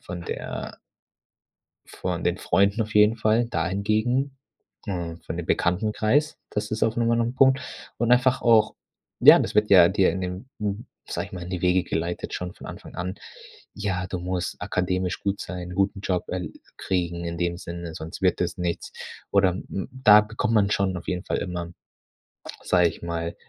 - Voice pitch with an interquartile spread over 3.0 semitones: Yes, average, 3.4 semitones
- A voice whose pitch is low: Yes, very low, 95 Hz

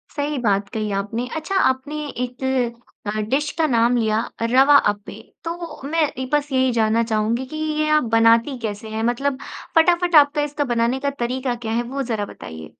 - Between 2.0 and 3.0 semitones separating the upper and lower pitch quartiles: No, average, 4.4 semitones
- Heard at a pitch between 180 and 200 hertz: No, very high, 250 Hz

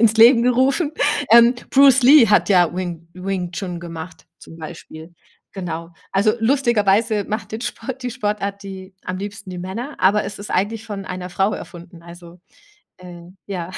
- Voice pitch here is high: Yes, high, 195 Hz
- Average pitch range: Yes, average, 4.3 semitones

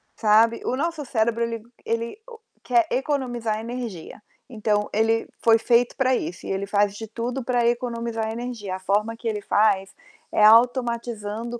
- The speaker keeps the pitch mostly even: Yes, narrow, 2.3 semitones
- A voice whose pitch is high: Yes, high, 230 Hz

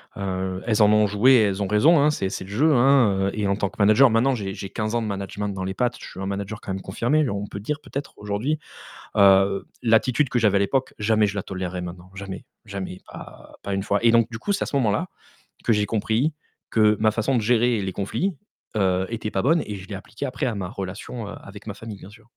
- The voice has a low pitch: Yes, low, 105 Hz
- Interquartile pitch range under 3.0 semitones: No, average, 3.3 semitones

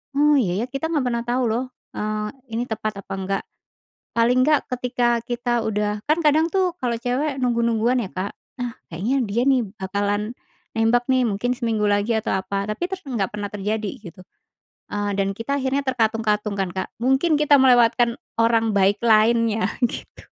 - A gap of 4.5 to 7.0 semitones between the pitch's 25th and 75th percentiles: No, average, 3.4 semitones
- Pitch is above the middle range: Yes, high, 230 Hz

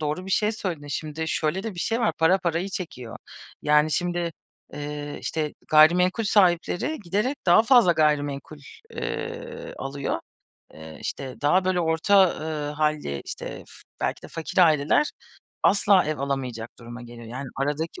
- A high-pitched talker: No, medium, 160 Hz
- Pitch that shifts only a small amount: No, average, 4.3 semitones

